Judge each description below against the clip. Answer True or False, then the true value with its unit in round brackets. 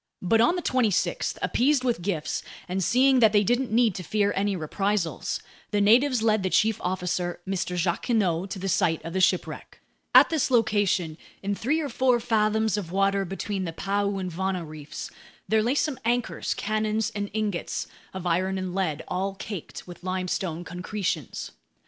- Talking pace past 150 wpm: True (175 wpm)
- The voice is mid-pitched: False (200 Hz)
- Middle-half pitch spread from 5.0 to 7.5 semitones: False (3.4 semitones)